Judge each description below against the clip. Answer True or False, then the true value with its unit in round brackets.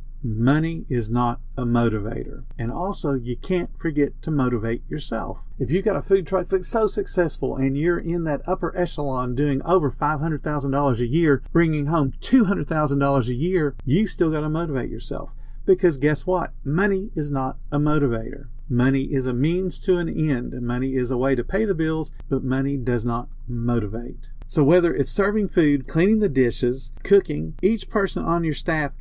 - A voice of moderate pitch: True (145 Hz)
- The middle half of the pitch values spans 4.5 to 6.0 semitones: True (5.3 semitones)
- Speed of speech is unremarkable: True (180 wpm)